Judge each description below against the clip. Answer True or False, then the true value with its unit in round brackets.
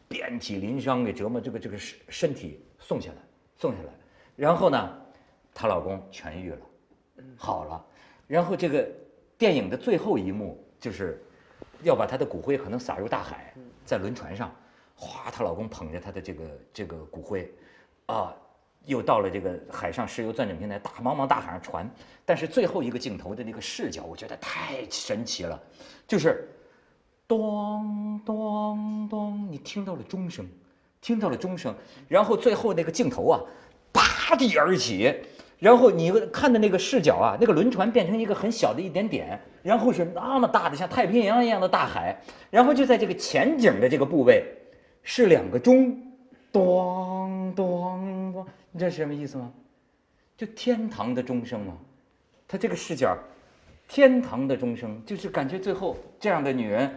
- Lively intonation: True (6.1 semitones)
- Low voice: False (200 Hz)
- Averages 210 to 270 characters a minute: True (255 characters per minute)